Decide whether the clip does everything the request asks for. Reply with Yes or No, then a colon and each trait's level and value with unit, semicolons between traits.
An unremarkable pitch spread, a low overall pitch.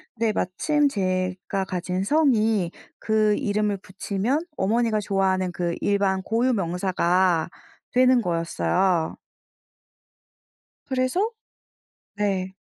No: average, 3.7 semitones; high, 195 Hz